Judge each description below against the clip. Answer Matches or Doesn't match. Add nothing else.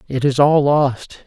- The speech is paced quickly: Doesn't match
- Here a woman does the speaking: Doesn't match